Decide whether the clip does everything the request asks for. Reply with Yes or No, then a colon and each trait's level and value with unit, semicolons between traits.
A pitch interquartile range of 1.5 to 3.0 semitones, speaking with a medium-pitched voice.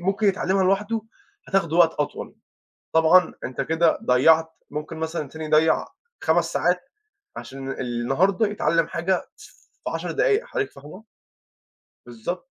No: average, 3.9 semitones; medium, 165 Hz